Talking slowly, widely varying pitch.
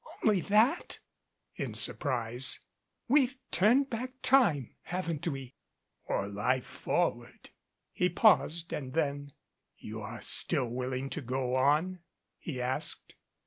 Yes: slow, 130 wpm; wide, 7.3 semitones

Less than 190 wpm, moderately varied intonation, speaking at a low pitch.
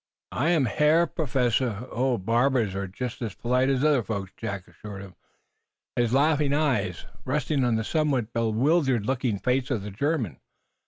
Yes: average, 170 wpm; average, 4.6 semitones; low, 125 Hz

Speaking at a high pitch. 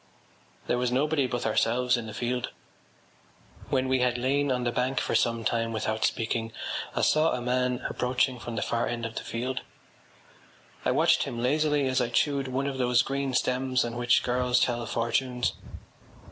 No: low, 125 Hz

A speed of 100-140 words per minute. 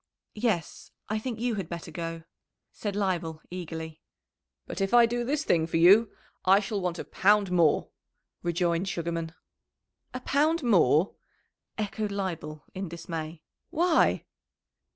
Yes: slow, 135 wpm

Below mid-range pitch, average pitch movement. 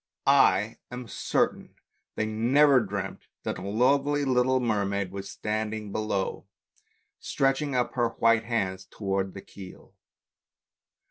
Yes: low, 110 Hz; average, 4.1 semitones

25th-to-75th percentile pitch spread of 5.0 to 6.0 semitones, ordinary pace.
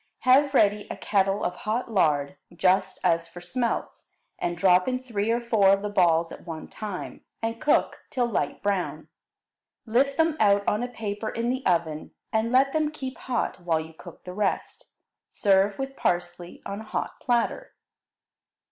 Yes: average, 5.3 semitones; average, 175 wpm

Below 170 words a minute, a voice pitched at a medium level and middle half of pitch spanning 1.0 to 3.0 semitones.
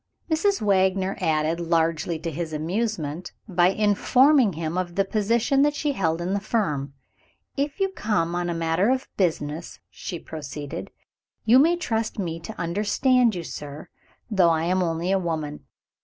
No: average, 160 wpm; medium, 180 Hz; average, 5.1 semitones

